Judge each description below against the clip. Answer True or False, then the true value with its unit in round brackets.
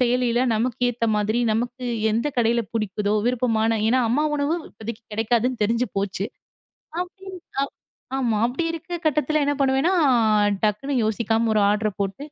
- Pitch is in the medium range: False (235 Hz)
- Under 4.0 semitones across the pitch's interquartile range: True (3.4 semitones)